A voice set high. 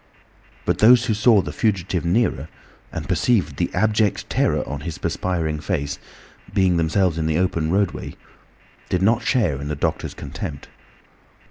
No: very low, 90 Hz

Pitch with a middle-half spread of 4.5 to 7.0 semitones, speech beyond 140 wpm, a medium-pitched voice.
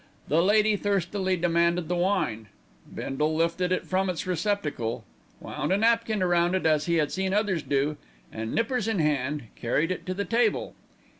Yes: average, 4.8 semitones; average, 170 wpm; medium, 180 Hz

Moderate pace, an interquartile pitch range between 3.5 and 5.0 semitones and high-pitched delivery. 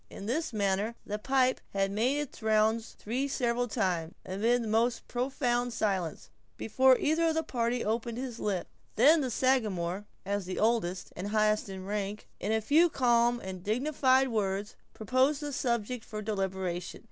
Yes: average, 165 wpm; average, 4.0 semitones; high, 225 Hz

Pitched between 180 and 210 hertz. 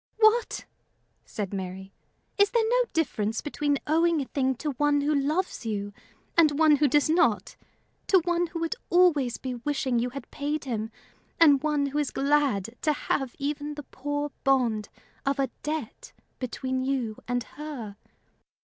No: very high, 285 Hz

